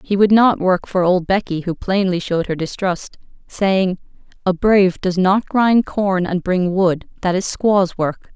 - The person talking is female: Yes, female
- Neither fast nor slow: Yes, average, 170 wpm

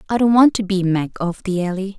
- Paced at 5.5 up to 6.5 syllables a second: Yes, 5.6 syllables/s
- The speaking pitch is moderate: No, high, 195 Hz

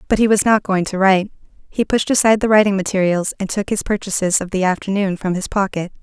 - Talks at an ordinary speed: No, fast, 230 wpm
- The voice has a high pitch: Yes, high, 195 Hz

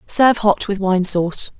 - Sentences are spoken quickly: No, average, 190 wpm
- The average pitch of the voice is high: Yes, high, 200 Hz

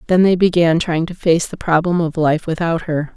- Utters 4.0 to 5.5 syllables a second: Yes, 5.1 syllables/s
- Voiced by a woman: Yes, female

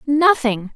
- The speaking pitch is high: Yes, very high, 265 Hz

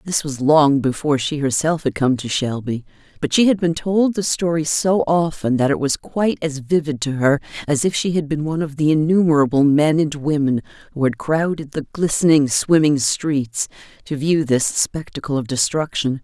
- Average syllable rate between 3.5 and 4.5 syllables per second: No, 5.0 syllables/s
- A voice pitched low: No, medium, 150 Hz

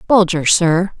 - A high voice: No, medium, 180 Hz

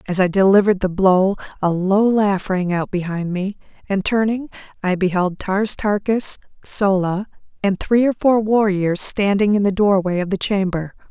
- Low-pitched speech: No, high, 195 Hz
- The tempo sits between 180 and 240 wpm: No, average, 165 wpm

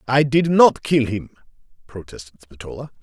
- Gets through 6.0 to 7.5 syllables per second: No, 5.1 syllables/s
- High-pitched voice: No, low, 125 Hz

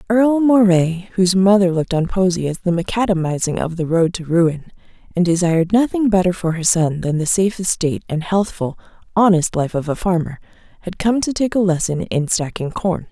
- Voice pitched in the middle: Yes, medium, 180 Hz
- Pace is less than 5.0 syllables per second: No, 5.6 syllables/s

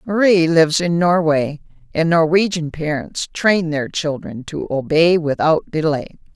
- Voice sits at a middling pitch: Yes, medium, 160 Hz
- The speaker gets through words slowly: Yes, slow, 130 wpm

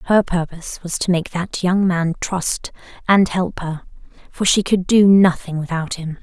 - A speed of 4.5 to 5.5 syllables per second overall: No, 4.3 syllables/s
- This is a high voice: No, medium, 180 Hz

